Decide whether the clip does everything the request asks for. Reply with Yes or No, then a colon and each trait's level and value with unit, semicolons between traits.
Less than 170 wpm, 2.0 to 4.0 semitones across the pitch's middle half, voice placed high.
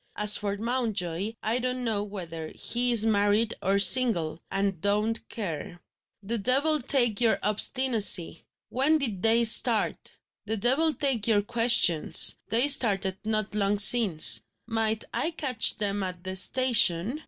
Yes: average, 140 wpm; average, 3.6 semitones; high, 220 Hz